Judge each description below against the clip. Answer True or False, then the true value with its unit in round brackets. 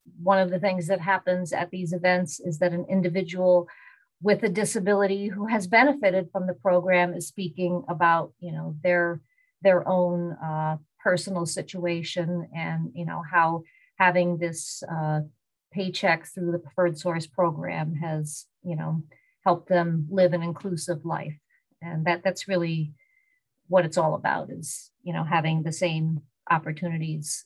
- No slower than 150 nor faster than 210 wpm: True (155 wpm)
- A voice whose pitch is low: False (175 Hz)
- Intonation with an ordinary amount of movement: False (2.1 semitones)